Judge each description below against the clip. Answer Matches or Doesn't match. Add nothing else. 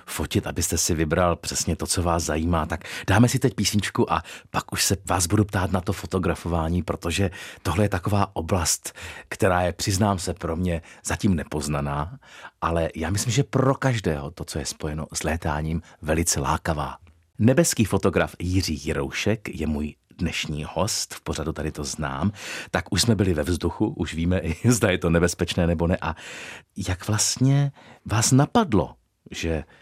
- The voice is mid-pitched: Doesn't match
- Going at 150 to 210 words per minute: Matches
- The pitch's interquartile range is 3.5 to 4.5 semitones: Matches